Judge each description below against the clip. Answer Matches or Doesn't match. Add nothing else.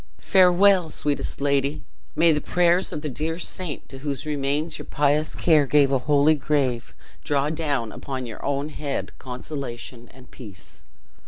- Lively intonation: Doesn't match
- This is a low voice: Doesn't match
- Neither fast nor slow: Matches